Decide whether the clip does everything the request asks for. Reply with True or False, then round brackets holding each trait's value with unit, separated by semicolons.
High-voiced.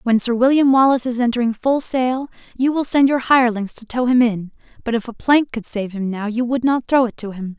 True (240 Hz)